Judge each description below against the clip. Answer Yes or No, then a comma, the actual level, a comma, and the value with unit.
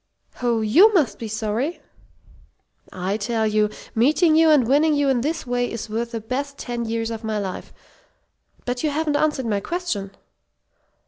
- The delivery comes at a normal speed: Yes, average, 170 wpm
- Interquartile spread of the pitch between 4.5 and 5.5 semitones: Yes, average, 5.1 semitones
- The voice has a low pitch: No, high, 240 Hz